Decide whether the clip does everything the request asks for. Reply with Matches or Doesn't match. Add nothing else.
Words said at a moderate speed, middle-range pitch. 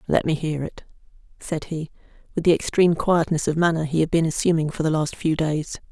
Doesn't match